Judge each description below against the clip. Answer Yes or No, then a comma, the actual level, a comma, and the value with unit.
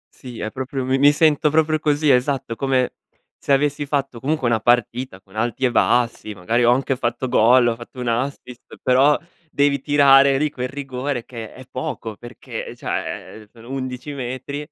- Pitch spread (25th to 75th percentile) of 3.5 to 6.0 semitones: No, average, 2.9 semitones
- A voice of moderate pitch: No, low, 130 Hz